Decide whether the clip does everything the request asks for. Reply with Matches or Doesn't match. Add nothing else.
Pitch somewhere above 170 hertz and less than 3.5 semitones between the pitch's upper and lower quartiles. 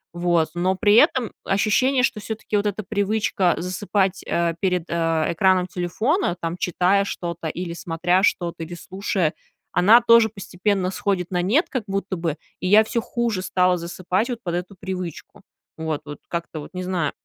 Matches